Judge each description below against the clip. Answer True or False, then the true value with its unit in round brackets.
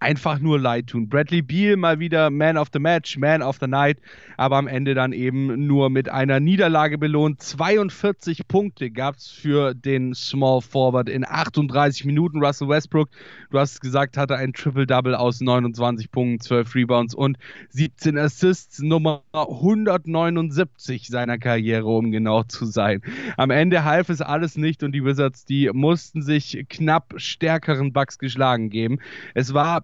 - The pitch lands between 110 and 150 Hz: True (140 Hz)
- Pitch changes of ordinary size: True (3.4 semitones)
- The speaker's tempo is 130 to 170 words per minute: True (160 wpm)